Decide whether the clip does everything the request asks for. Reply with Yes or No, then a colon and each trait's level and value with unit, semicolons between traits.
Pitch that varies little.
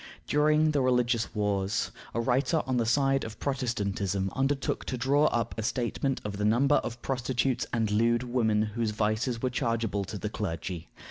No: average, 3.7 semitones